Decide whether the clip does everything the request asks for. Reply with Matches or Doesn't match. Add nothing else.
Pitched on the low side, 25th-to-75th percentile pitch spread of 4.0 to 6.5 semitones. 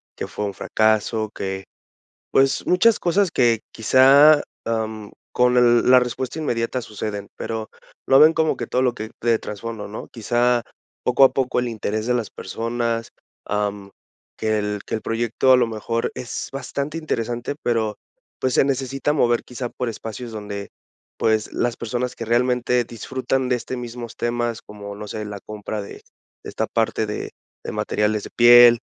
Doesn't match